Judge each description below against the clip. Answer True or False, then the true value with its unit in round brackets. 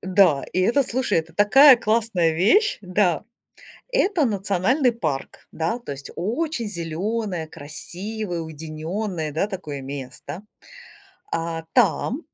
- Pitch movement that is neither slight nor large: False (6.0 semitones)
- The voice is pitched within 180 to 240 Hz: True (185 Hz)